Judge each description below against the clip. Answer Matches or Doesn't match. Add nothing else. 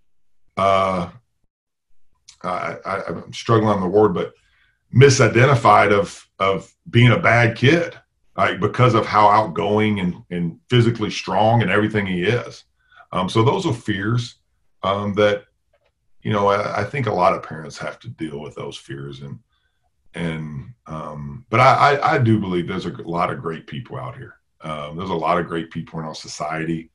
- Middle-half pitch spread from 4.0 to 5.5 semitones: Matches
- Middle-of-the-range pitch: Doesn't match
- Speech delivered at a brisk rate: Doesn't match